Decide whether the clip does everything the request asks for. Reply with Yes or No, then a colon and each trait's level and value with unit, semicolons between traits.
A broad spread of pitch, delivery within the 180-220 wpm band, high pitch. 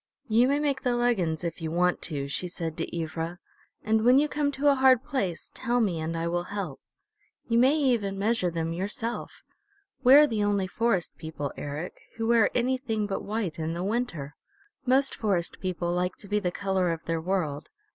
Yes: wide, 6.2 semitones; average, 195 wpm; high, 195 Hz